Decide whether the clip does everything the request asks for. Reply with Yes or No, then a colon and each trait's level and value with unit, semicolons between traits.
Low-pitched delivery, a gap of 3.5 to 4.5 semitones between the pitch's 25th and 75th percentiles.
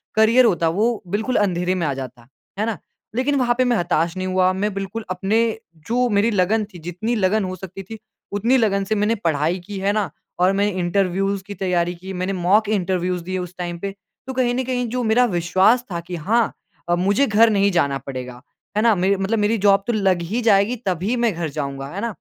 No: high, 195 Hz; average, 3.8 semitones